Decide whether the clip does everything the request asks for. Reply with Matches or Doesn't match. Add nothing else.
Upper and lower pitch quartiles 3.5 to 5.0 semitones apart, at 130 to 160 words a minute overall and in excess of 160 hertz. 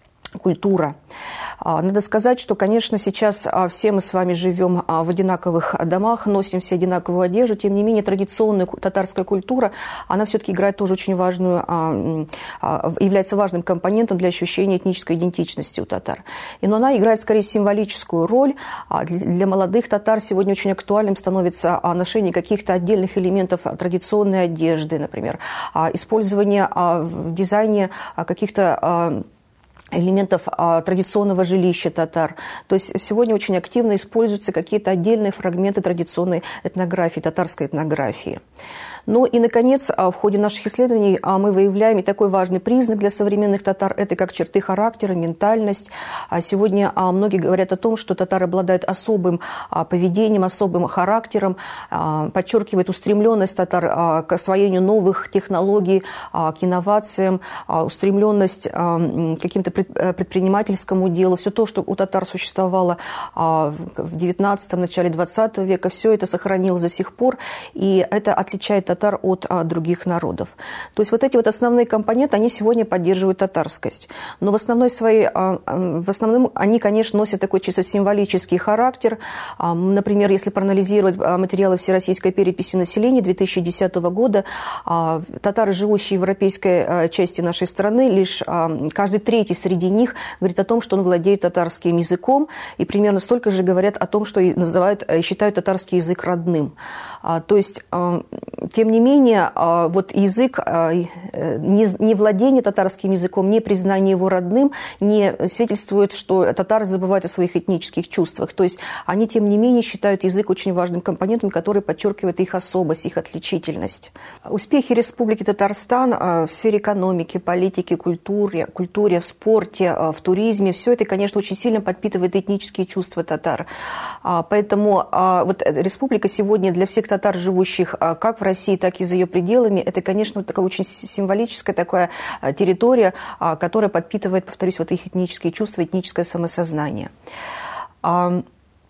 Doesn't match